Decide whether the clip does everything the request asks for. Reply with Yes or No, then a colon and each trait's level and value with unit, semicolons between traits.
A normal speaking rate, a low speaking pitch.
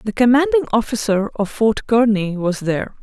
No: average, 160 wpm; high, 225 Hz